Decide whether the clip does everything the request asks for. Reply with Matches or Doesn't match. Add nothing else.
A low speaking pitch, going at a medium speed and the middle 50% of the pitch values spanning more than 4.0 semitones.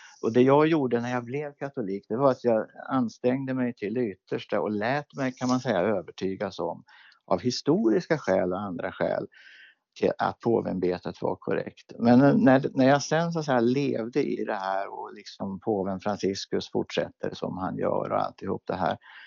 Matches